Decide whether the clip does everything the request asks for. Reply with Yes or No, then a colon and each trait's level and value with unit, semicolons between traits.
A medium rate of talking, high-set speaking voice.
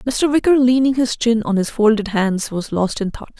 No: fast, 230 wpm; high, 230 Hz